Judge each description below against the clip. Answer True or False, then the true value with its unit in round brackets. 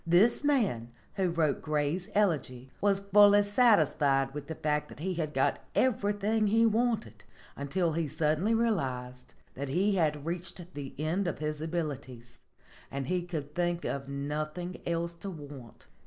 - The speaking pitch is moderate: True (165 Hz)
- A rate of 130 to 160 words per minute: True (155 wpm)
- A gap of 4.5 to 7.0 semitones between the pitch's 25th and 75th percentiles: True (5.6 semitones)